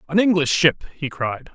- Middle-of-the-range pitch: Yes, medium, 160 Hz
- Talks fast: No, average, 195 wpm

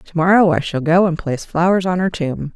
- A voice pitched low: No, medium, 170 Hz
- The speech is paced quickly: Yes, fast, 260 wpm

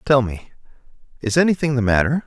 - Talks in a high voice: No, low, 130 Hz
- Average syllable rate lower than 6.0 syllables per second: No, 6.2 syllables/s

